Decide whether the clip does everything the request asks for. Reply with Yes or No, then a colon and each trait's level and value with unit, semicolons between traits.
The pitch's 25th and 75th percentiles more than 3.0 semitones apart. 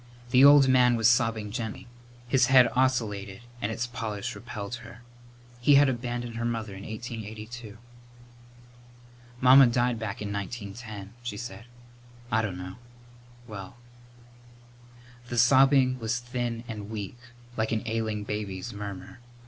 No: narrow, 2.6 semitones